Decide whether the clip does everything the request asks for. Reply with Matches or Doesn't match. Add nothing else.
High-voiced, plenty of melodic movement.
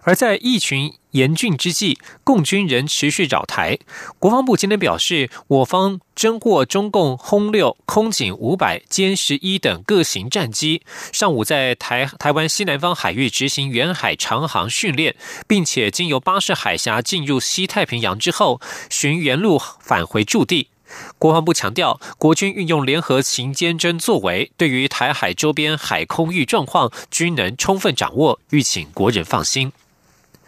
Doesn't match